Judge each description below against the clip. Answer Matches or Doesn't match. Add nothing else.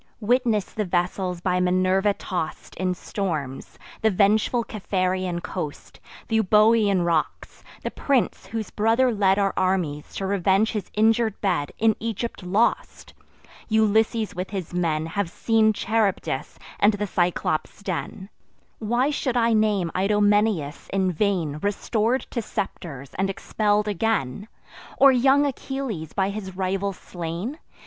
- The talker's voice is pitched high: Matches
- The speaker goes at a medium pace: Doesn't match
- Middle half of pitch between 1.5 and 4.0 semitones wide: Matches